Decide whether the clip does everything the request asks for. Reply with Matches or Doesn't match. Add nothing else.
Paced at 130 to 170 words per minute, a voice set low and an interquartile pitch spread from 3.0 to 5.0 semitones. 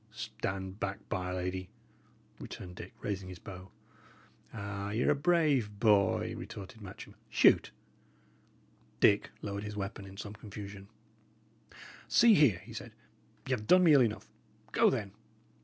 Doesn't match